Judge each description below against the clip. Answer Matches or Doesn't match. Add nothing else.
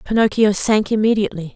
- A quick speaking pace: Doesn't match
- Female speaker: Matches